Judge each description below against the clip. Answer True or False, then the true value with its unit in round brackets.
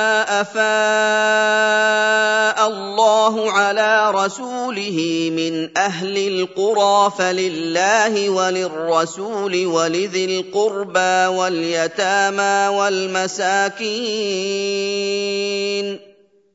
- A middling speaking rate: False (45 wpm)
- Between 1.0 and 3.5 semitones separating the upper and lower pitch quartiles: True (2.4 semitones)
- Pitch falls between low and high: False (200 Hz)